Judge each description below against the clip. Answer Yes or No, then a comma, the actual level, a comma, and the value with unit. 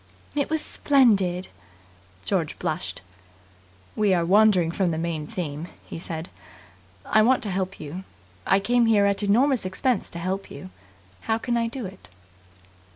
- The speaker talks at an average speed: Yes, average, 155 wpm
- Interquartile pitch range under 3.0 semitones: No, average, 4.7 semitones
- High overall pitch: Yes, high, 195 Hz